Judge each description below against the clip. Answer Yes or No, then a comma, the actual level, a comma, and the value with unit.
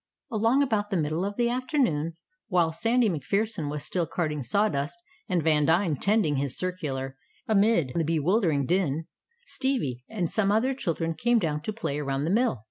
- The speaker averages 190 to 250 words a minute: No, average, 165 wpm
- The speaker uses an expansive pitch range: Yes, wide, 6.5 semitones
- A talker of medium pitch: Yes, medium, 175 Hz